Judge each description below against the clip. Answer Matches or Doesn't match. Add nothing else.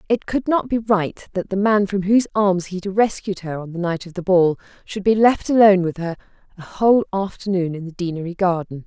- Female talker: Matches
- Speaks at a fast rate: Matches